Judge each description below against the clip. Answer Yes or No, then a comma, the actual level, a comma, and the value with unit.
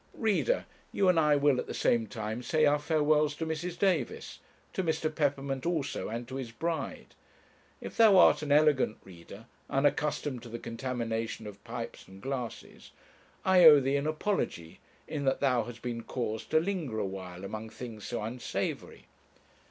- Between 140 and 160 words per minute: No, average, 170 wpm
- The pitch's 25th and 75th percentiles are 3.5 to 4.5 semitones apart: No, average, 5.1 semitones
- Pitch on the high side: No, low, 135 Hz